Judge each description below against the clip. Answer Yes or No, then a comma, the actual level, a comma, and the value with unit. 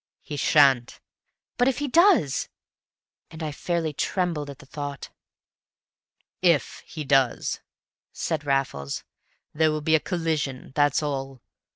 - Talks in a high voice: No, medium, 150 Hz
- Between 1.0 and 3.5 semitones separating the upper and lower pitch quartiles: Yes, average, 3.1 semitones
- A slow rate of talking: Yes, slow, 130 wpm